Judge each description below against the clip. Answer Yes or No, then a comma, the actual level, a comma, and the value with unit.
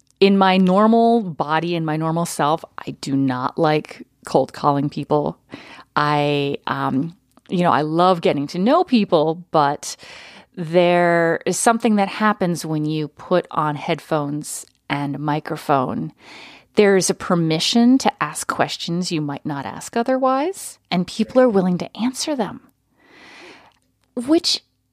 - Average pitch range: No, wide, 5.9 semitones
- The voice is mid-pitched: Yes, medium, 175 Hz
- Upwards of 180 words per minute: No, average, 140 wpm